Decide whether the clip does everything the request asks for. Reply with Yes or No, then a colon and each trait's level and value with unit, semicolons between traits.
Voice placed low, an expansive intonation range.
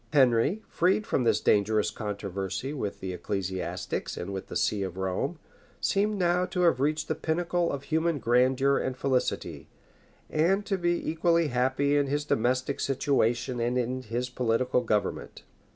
Yes: low, 130 Hz; wide, 5.8 semitones